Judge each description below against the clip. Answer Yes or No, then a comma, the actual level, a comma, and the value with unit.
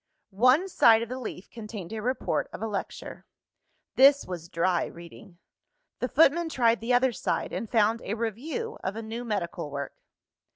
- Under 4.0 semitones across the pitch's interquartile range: No, average, 4.5 semitones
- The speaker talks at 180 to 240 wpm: No, average, 170 wpm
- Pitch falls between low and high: No, high, 225 Hz